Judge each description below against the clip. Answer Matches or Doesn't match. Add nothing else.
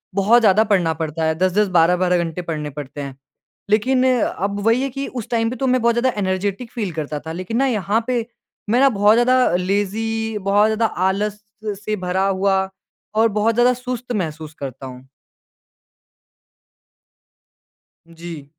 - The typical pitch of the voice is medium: Doesn't match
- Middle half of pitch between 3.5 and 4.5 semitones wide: Doesn't match